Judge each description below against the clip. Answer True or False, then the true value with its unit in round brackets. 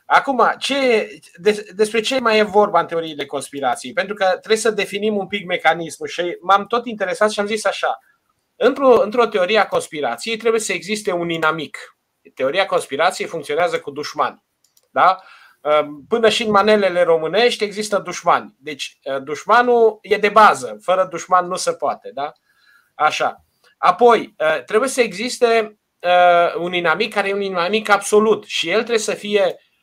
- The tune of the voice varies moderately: True (4.5 semitones)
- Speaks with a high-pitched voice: True (205 Hz)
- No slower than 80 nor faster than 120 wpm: False (155 wpm)